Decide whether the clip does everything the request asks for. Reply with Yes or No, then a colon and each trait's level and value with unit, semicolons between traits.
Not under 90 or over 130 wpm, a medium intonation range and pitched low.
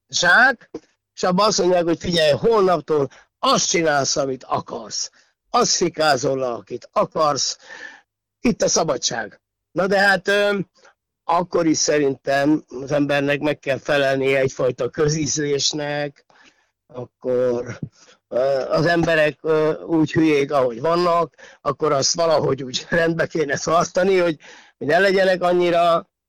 No: average, 115 wpm; average, 3.9 semitones; medium, 155 Hz